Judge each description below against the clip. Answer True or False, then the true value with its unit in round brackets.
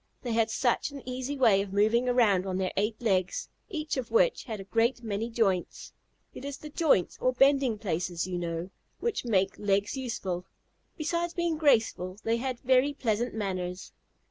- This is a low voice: False (230 Hz)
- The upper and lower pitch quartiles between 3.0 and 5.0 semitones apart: False (5.4 semitones)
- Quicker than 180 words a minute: False (175 wpm)